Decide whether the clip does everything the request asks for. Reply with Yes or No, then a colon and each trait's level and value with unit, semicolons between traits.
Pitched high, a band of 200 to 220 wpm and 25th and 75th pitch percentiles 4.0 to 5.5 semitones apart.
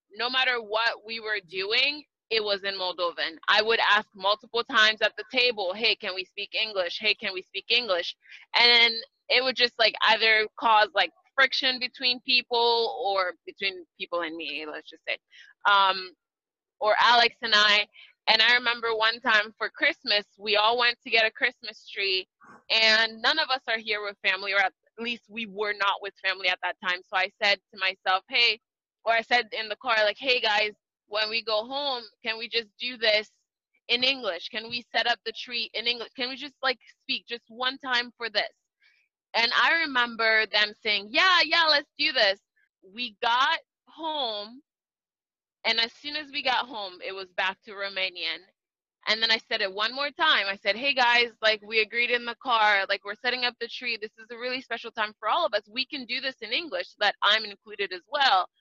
No: high, 225 Hz; fast, 205 wpm; average, 3.4 semitones